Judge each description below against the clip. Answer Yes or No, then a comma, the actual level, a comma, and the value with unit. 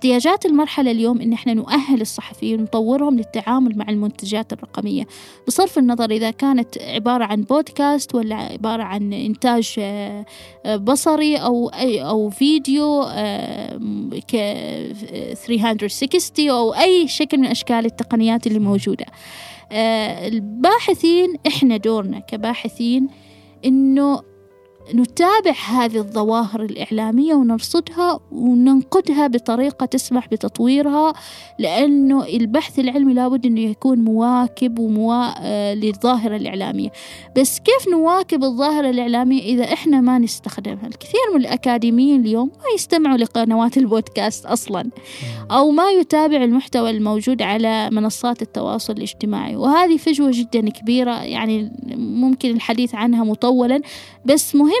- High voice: Yes, high, 245 Hz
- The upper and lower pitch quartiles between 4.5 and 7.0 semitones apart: No, average, 3.7 semitones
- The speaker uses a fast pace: No, average, 105 wpm